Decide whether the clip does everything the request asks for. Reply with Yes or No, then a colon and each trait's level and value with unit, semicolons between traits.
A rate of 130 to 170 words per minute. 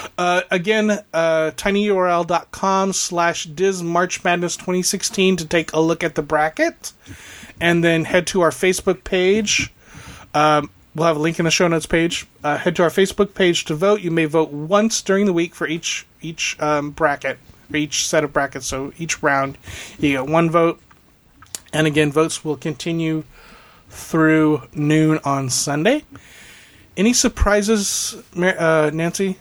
Yes: average, 155 wpm